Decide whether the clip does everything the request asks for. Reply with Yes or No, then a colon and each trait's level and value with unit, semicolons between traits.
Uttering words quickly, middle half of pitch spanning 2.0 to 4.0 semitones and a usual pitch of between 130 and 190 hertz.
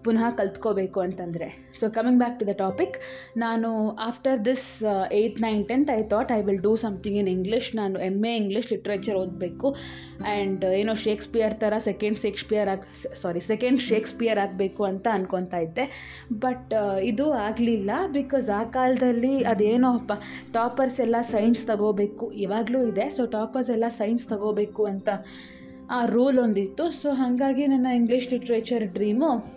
No: fast, 145 wpm; average, 3.0 semitones; high, 220 Hz